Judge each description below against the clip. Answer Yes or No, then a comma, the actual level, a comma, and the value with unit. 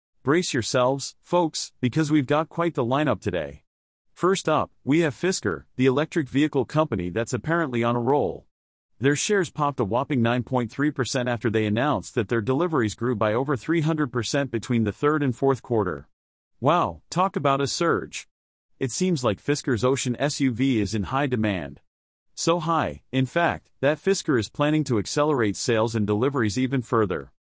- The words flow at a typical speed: Yes, average, 165 wpm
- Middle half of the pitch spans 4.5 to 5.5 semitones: Yes, average, 4.8 semitones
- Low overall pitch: Yes, low, 130 Hz